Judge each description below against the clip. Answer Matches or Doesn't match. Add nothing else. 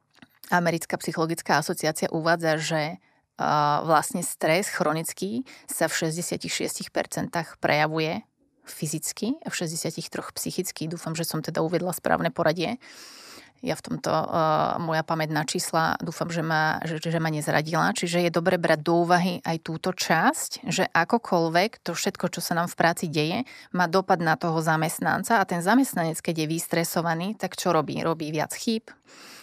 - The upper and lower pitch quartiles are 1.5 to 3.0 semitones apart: Matches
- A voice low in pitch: Doesn't match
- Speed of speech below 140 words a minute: Doesn't match